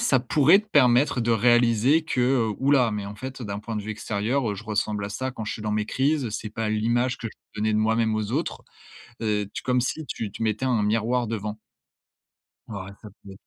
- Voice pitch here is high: No, low, 115 Hz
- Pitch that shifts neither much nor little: Yes, average, 3.1 semitones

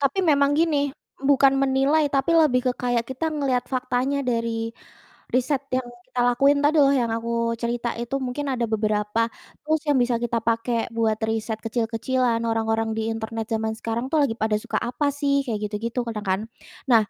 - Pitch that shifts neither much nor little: Yes, average, 3.3 semitones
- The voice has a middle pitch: No, high, 240 Hz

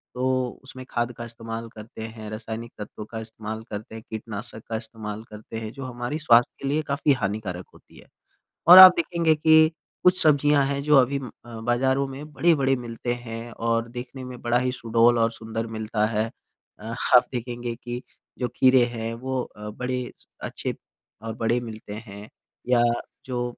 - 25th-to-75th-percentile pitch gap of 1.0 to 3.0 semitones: Yes, average, 2.7 semitones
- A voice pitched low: Yes, low, 120 Hz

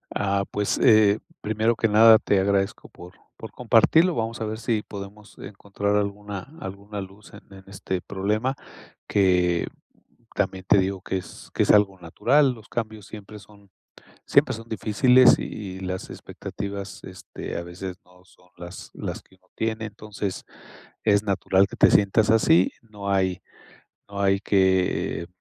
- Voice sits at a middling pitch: No, low, 100 Hz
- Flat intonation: Yes, narrow, 2.2 semitones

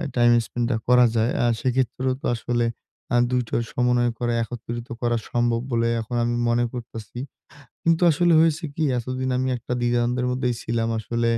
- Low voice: Yes, low, 120 Hz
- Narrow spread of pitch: Yes, narrow, 1.2 semitones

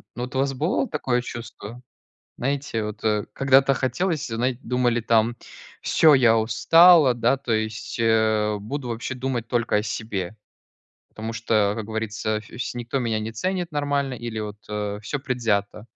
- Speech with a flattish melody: No, average, 3.4 semitones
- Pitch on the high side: No, low, 115 Hz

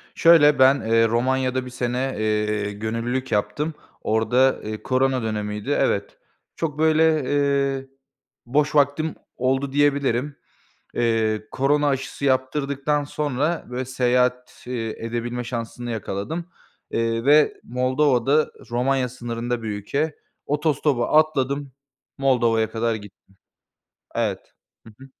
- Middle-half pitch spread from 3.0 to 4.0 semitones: Yes, average, 3.6 semitones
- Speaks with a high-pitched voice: No, low, 130 Hz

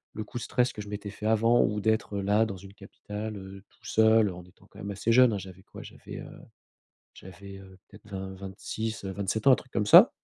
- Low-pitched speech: Yes, low, 105 Hz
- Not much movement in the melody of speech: Yes, narrow, 2.2 semitones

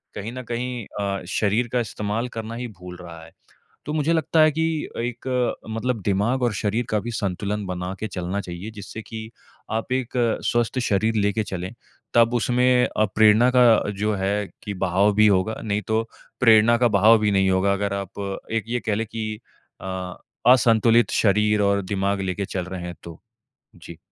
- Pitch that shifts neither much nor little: Yes, average, 3.0 semitones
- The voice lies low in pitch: Yes, low, 105 Hz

